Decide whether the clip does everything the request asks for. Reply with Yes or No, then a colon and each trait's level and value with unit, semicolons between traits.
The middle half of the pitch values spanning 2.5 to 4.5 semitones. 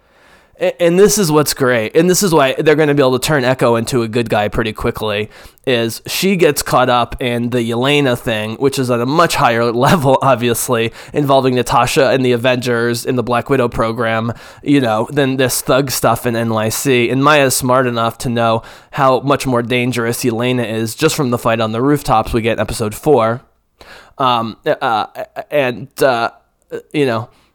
Yes: average, 3.1 semitones